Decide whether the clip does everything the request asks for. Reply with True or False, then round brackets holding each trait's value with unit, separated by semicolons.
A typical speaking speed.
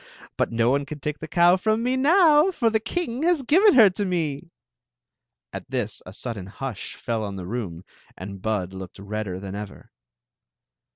True (180 wpm)